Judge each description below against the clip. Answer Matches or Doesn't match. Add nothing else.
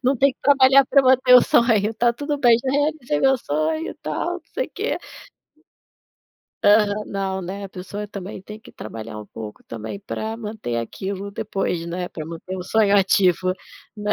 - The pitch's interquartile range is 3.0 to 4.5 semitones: Doesn't match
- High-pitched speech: Matches